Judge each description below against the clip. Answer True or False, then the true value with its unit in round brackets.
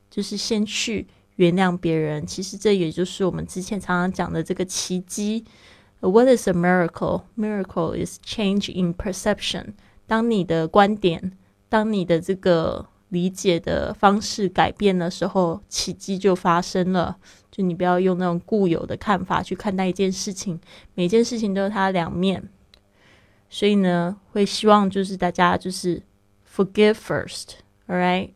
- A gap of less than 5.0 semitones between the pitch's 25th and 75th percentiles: True (2.5 semitones)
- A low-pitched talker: False (185 Hz)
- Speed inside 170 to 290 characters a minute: False (325 characters per minute)